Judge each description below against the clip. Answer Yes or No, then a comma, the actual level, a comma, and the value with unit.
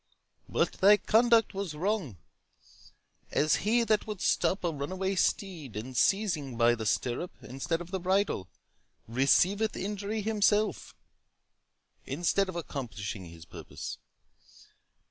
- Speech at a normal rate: No, slow, 120 wpm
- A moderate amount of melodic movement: No, wide, 7.4 semitones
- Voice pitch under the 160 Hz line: No, medium, 185 Hz